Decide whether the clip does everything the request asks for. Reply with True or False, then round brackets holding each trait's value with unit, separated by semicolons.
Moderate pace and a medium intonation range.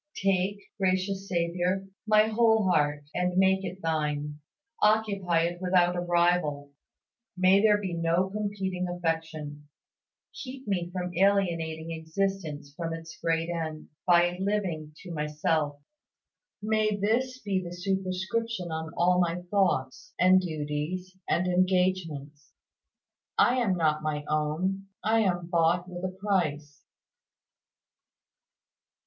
False (120 wpm; 3.2 semitones)